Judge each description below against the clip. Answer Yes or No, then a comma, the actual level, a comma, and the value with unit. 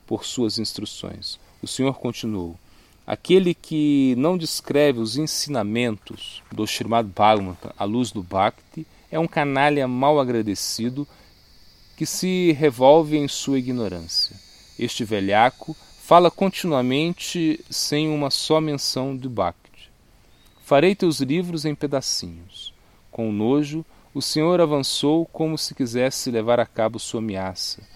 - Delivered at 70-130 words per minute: Yes, average, 125 wpm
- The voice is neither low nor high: No, low, 130 Hz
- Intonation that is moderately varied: No, wide, 6.3 semitones